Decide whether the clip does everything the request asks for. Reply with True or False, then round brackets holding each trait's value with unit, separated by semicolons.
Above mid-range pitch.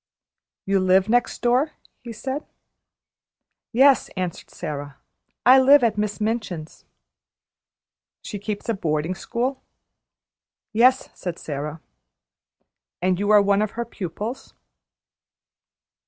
True (210 Hz)